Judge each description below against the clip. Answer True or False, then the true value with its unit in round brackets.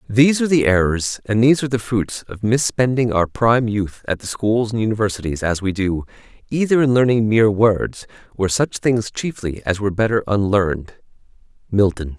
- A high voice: False (110 Hz)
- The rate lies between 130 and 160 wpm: False (170 wpm)